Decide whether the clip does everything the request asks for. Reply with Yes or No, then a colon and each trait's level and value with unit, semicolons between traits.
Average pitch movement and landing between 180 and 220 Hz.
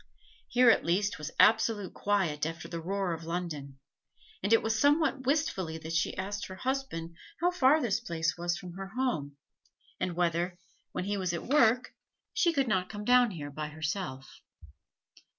No: wide, 6.4 semitones; high, 190 Hz